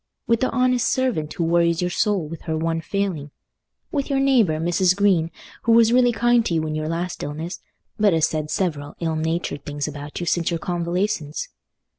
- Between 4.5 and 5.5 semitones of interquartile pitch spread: Yes, average, 4.9 semitones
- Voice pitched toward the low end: No, medium, 170 Hz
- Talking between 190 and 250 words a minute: Yes, average, 195 wpm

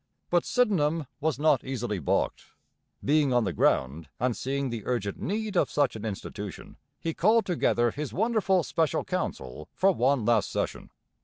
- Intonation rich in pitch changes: Yes, wide, 7.0 semitones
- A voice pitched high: No, medium, 140 Hz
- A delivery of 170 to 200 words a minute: No, average, 160 wpm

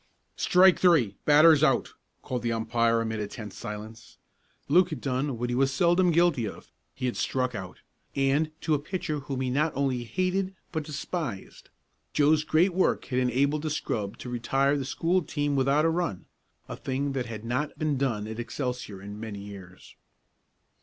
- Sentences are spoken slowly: No, average, 180 wpm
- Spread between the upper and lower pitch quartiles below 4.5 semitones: No, average, 5.0 semitones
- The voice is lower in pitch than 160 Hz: Yes, low, 135 Hz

